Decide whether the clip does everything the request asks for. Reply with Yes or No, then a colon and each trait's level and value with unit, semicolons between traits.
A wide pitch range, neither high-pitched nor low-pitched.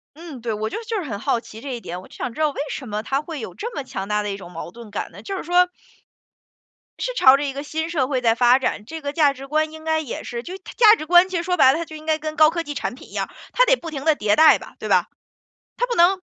No: wide, 5.8 semitones; very high, 295 Hz